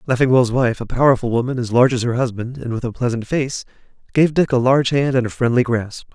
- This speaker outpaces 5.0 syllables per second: Yes, 6.2 syllables/s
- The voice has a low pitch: Yes, low, 125 Hz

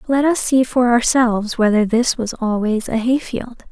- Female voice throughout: Yes, female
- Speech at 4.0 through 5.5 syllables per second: Yes, 4.9 syllables/s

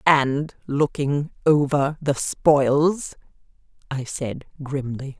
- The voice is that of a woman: Yes, female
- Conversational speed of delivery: No, slow, 90 wpm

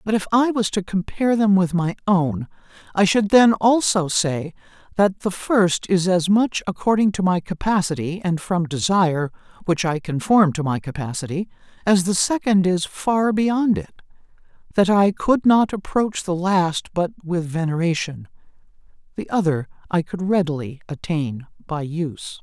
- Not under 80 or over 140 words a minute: No, average, 160 wpm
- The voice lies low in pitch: No, medium, 185 Hz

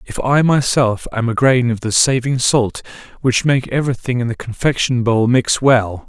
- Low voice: Yes, low, 125 Hz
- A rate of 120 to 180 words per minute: No, average, 190 wpm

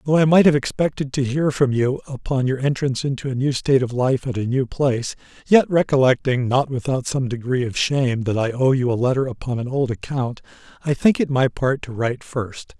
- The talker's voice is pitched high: No, low, 130 Hz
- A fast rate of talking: Yes, fast, 225 wpm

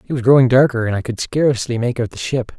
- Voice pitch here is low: Yes, low, 125 Hz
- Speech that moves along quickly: Yes, fast, 280 wpm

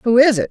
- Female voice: Yes, female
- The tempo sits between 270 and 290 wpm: No, fast, 360 wpm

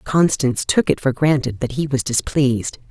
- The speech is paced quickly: No, average, 185 wpm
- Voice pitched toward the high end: No, low, 135 Hz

